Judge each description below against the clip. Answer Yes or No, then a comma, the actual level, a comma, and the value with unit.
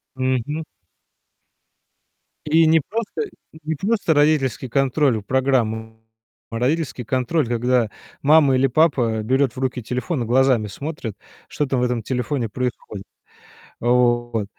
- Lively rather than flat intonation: No, average, 3.6 semitones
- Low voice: Yes, low, 130 Hz